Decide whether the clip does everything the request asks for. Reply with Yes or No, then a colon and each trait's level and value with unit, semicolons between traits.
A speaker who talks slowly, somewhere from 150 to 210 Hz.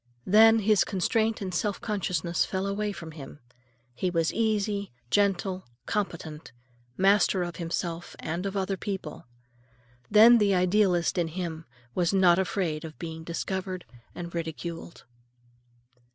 Yes: slow, 130 wpm; medium, 185 Hz